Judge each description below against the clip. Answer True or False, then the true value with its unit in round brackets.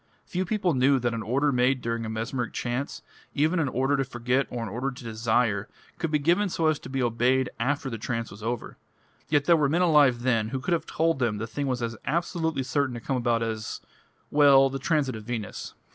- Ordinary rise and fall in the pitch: True (3.8 semitones)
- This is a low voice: True (130 Hz)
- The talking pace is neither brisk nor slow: False (225 wpm)